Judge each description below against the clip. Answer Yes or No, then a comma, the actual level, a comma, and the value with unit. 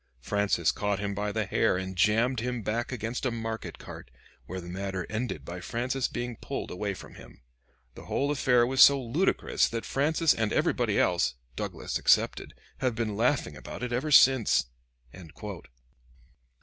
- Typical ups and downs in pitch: Yes, average, 4.0 semitones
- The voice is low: Yes, low, 115 Hz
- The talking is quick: No, average, 160 wpm